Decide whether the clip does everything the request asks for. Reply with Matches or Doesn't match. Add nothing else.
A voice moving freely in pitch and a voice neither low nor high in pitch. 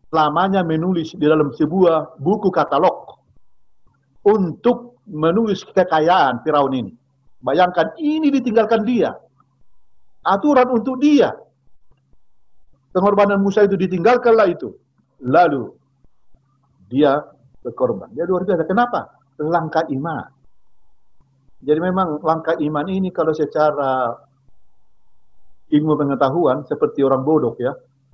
Matches